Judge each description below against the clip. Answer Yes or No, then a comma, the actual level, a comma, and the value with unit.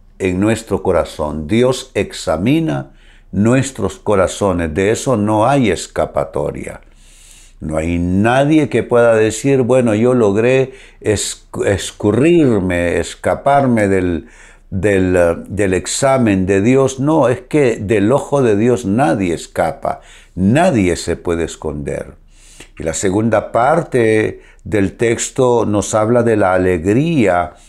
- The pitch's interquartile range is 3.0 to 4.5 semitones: No, average, 5.3 semitones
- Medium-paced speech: No, slow, 115 wpm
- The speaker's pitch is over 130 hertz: No, low, 110 Hz